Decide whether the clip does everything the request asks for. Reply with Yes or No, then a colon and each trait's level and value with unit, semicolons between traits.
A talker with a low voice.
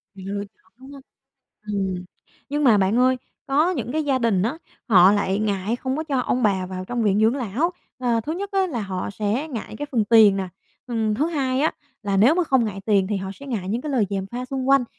No: high, 230 Hz